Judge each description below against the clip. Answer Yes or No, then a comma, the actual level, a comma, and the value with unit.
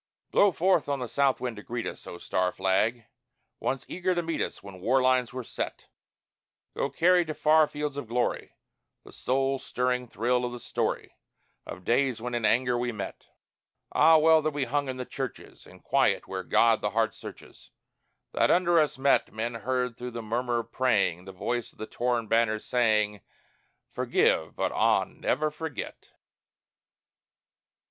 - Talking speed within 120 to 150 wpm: No, average, 175 wpm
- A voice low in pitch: Yes, low, 125 Hz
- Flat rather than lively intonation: No, average, 3.8 semitones